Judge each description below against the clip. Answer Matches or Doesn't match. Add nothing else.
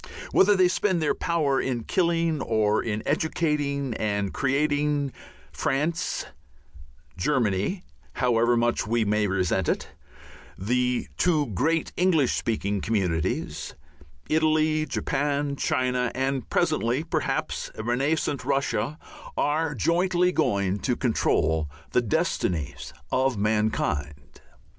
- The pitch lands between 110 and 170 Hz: Matches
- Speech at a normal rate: Doesn't match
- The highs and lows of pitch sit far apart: Matches